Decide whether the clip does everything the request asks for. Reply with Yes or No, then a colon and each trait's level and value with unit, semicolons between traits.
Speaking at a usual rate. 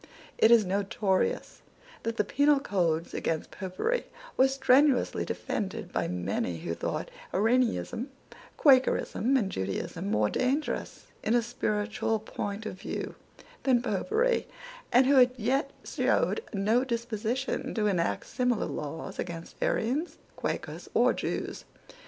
No: slow, 120 wpm